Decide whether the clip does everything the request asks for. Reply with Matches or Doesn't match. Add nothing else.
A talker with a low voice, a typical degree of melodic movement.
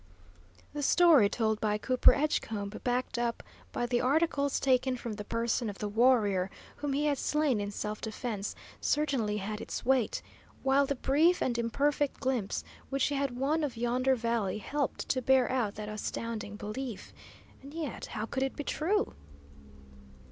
Doesn't match